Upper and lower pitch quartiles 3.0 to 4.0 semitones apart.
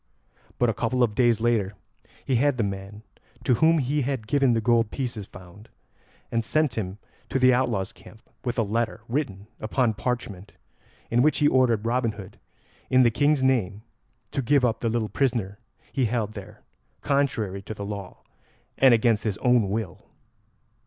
Yes: average, 3.5 semitones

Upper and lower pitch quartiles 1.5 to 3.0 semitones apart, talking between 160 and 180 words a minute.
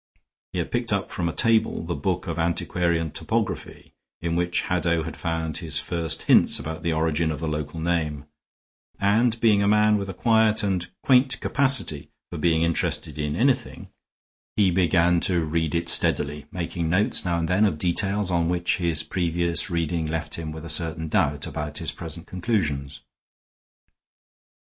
Yes: narrow, 2.6 semitones; average, 170 wpm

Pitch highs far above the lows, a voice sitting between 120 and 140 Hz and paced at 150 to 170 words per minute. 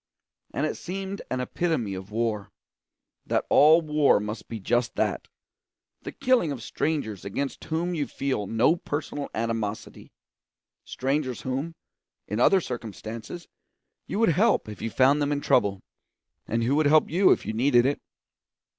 Yes: wide, 5.7 semitones; low, 135 Hz; average, 155 wpm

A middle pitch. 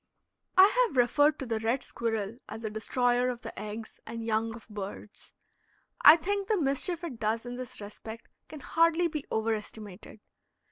No: high, 235 Hz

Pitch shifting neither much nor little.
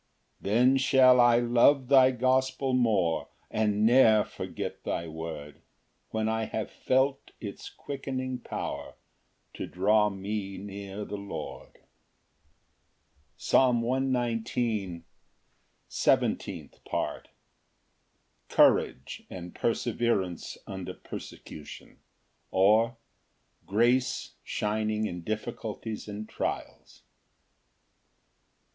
Yes: average, 3.9 semitones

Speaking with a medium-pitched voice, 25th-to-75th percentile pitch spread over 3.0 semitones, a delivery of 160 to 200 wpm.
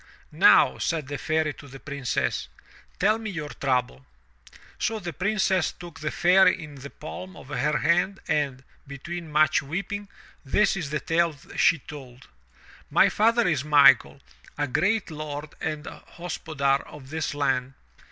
No: medium, 155 Hz; average, 3.9 semitones; average, 150 wpm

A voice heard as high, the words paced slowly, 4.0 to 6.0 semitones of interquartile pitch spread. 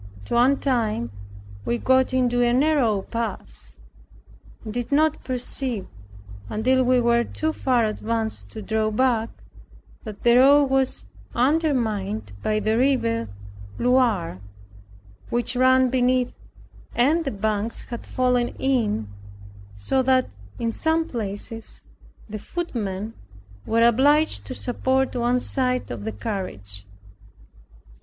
No: high, 240 Hz; slow, 120 wpm; average, 3.3 semitones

